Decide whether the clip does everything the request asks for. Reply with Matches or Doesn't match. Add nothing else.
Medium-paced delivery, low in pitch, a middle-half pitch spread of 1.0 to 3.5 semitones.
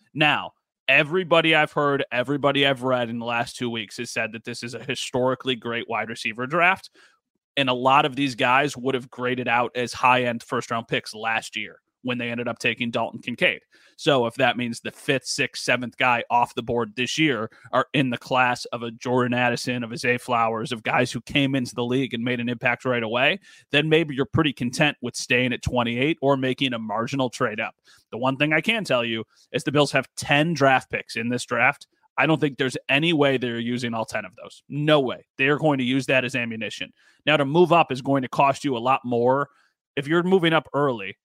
Doesn't match